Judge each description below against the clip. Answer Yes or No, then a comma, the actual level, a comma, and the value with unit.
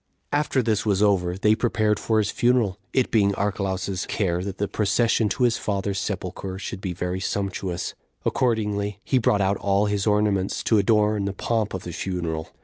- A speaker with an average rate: Yes, average, 185 wpm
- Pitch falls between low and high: No, low, 100 Hz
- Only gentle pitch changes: Yes, narrow, 2.2 semitones